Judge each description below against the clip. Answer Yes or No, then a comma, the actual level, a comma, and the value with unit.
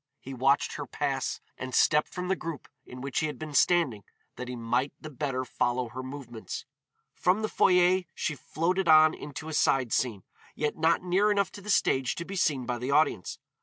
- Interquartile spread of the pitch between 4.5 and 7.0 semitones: Yes, average, 5.0 semitones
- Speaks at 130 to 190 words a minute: No, fast, 205 wpm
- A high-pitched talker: No, medium, 145 Hz